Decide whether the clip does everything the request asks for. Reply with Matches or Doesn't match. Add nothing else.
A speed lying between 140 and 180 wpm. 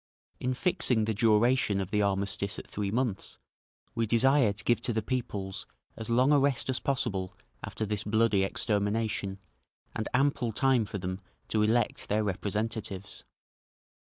Matches